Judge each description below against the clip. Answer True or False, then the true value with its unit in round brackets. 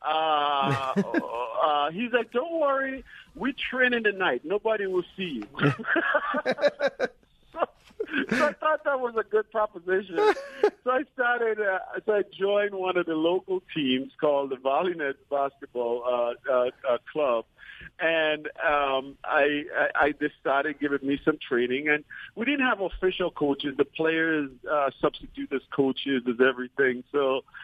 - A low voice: False (170 Hz)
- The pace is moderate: True (155 wpm)